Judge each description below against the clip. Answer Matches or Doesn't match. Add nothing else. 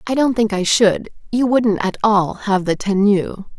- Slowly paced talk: Doesn't match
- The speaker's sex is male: Doesn't match